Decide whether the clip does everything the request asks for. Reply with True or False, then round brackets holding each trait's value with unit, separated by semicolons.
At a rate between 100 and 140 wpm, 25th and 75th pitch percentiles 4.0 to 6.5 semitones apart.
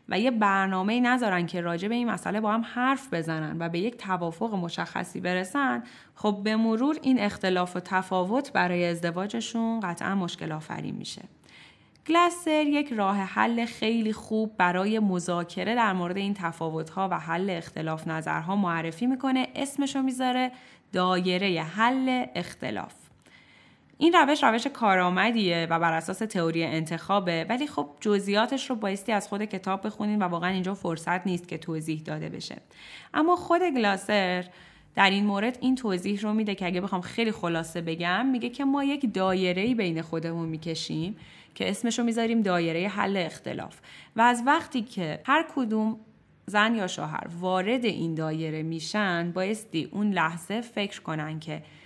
False (155 wpm; 5.0 semitones)